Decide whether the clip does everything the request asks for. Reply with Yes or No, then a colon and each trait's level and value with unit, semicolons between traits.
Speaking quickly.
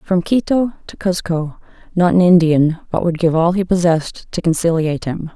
No: average, 180 wpm